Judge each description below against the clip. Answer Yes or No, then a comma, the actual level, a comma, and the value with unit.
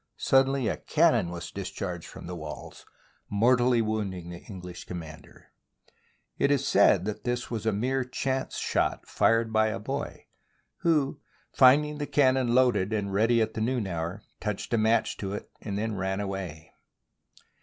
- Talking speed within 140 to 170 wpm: Yes, average, 160 wpm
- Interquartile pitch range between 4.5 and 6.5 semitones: Yes, average, 4.9 semitones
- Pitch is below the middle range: Yes, low, 110 Hz